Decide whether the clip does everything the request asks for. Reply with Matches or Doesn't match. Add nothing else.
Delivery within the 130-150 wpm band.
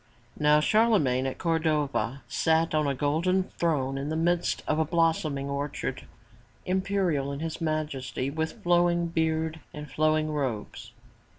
Matches